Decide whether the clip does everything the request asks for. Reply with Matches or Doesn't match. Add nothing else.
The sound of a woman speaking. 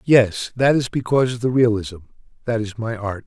Doesn't match